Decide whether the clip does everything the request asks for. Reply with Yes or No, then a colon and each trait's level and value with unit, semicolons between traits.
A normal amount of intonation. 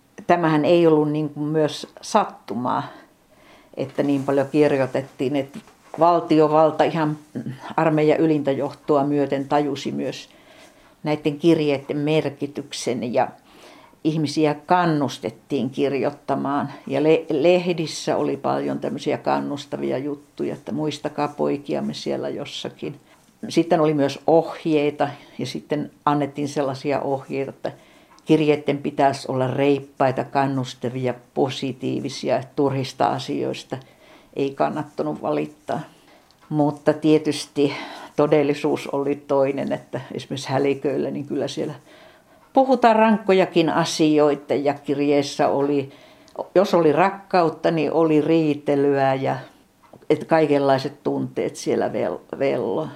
No: narrow, 2.1 semitones